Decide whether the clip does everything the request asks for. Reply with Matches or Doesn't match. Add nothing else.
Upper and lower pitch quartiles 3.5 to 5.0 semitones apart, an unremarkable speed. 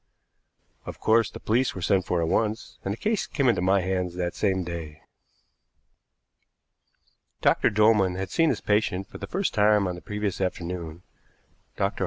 Doesn't match